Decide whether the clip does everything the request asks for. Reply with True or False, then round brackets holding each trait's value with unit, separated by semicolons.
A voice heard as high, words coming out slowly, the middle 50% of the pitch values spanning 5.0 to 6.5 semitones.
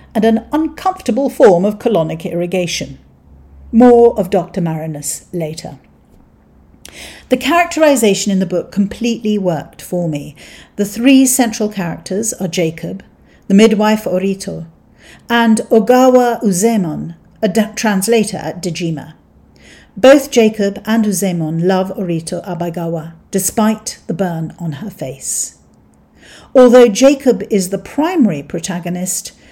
True (195 Hz; 115 wpm; 5.4 semitones)